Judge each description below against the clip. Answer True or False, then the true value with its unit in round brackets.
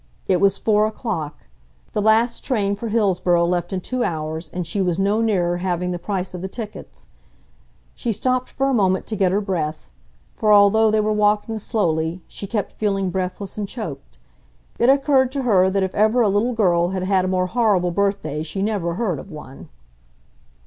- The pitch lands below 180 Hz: False (195 Hz)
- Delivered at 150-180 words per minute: False (190 wpm)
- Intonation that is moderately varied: True (3.4 semitones)